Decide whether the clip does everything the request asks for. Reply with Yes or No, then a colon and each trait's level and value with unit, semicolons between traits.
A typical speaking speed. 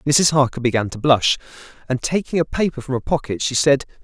No: fast, 210 wpm